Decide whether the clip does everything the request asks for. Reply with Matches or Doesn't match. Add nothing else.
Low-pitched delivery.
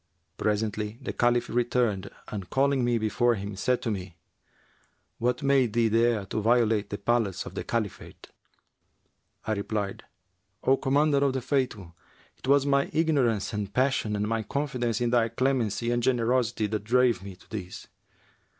Matches